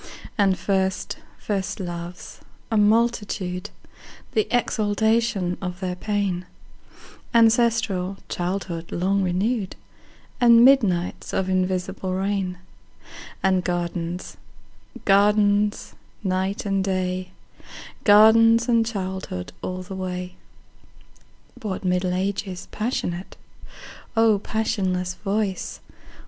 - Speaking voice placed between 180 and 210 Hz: Yes, high, 190 Hz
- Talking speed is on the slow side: Yes, slow, 75 wpm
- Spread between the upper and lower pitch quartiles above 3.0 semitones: No, average, 2.7 semitones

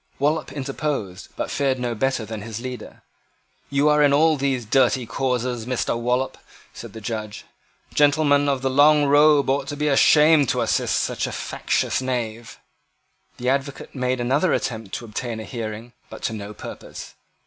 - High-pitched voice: No, low, 130 Hz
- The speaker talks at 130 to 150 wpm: No, average, 165 wpm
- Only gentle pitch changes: No, average, 3.5 semitones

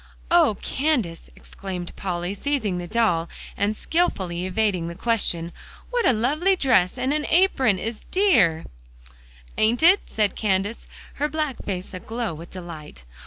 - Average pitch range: No, wide, 7.8 semitones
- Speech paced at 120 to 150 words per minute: Yes, average, 145 wpm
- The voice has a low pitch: No, high, 215 Hz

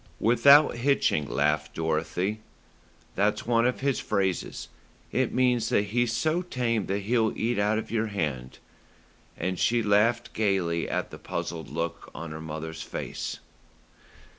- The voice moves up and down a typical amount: No, wide, 6.2 semitones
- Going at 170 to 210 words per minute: No, average, 140 wpm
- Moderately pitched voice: No, low, 105 Hz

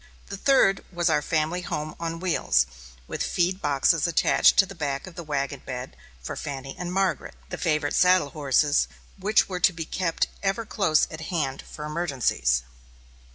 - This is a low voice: No, medium, 165 Hz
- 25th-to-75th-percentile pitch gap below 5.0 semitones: Yes, average, 4.1 semitones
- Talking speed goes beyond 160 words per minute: Yes, average, 170 wpm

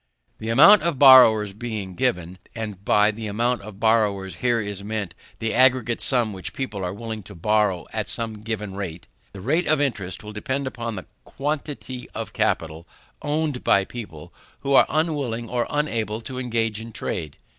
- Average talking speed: Yes, average, 175 wpm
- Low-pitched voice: Yes, low, 110 Hz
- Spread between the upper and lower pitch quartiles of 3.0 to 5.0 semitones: Yes, average, 4.1 semitones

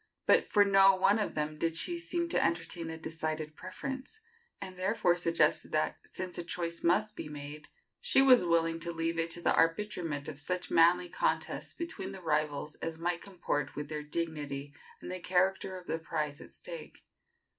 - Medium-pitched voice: Yes, medium, 170 Hz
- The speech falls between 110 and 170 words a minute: No, average, 185 wpm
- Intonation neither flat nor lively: Yes, average, 3.2 semitones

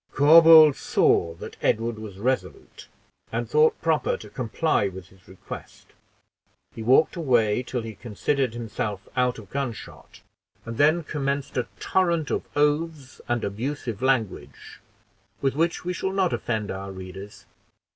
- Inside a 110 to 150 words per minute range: Yes, average, 140 wpm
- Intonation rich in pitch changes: Yes, wide, 6.2 semitones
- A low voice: Yes, low, 125 Hz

